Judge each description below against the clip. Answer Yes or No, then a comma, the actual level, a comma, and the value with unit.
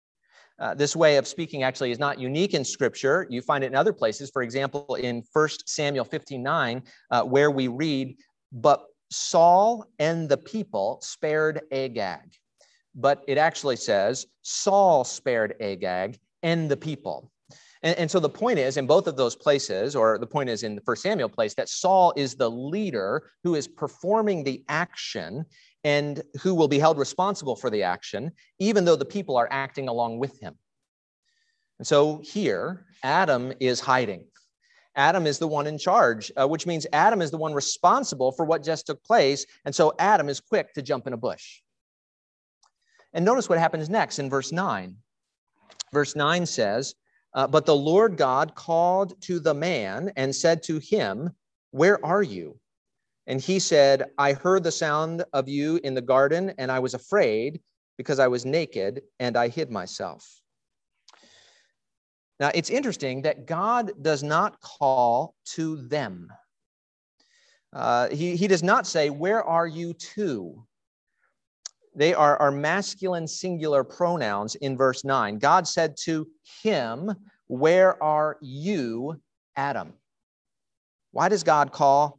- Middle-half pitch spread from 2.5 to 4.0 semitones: No, average, 4.6 semitones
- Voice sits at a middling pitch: Yes, medium, 150 Hz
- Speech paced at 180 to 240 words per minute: No, average, 160 wpm